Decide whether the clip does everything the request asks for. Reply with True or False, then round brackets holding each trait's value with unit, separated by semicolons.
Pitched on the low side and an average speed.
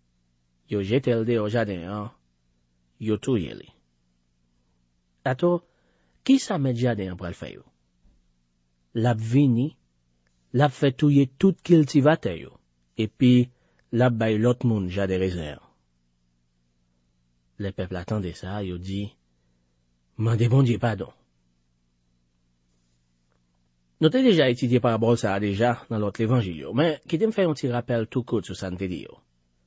False (95 Hz; 140 wpm)